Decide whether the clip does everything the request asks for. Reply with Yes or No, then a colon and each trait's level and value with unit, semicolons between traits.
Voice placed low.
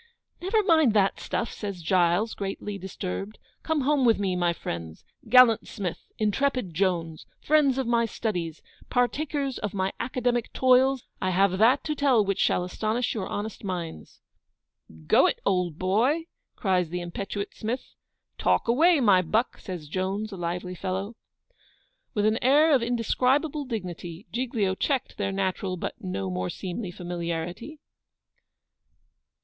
No: high, 205 Hz